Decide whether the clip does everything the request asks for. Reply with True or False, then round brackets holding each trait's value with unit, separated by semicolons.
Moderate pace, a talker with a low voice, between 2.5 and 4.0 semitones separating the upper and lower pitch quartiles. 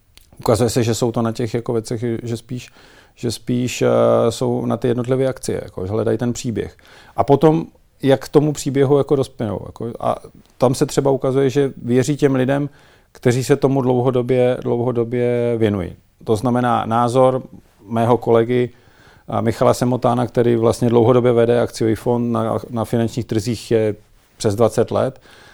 False (160 wpm; 120 Hz; 2.0 semitones)